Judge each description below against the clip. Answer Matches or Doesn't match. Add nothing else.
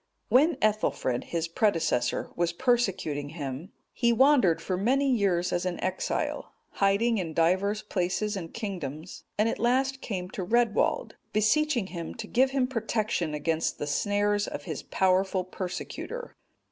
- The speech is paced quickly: Doesn't match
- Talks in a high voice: Matches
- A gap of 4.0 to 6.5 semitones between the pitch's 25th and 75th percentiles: Matches